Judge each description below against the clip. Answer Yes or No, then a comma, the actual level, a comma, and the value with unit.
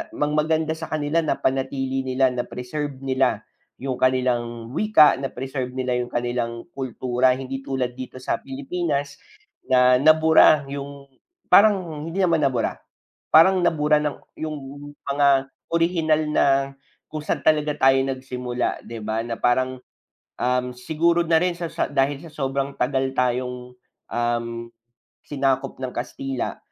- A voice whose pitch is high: No, low, 135 Hz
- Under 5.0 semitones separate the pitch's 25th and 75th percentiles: Yes, average, 3.3 semitones